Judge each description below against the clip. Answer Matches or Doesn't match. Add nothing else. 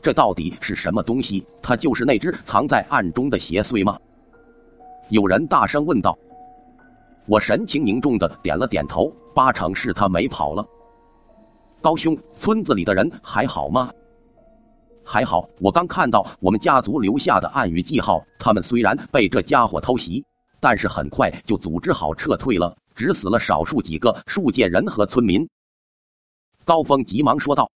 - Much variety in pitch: Matches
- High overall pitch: Matches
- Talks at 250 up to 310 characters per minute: Doesn't match